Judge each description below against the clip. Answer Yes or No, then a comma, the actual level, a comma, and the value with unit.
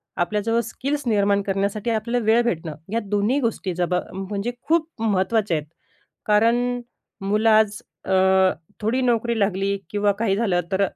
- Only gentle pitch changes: No, average, 3.0 semitones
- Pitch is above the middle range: Yes, high, 210 Hz